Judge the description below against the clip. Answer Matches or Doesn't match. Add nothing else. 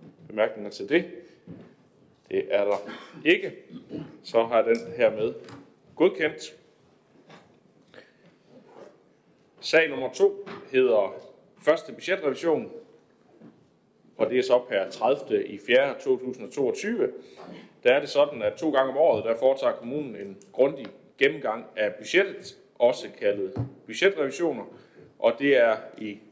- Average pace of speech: Doesn't match